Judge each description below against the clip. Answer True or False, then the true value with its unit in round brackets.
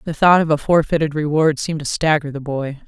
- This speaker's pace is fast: True (230 wpm)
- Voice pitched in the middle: True (150 Hz)